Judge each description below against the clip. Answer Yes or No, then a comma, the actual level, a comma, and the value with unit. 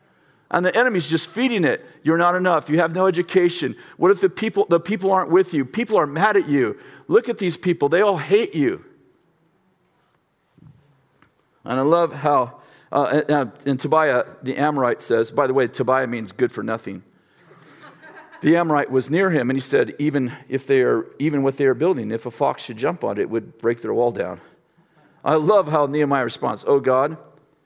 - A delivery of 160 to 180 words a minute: No, average, 195 wpm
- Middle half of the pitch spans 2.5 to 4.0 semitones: No, average, 4.9 semitones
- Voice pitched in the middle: Yes, medium, 150 Hz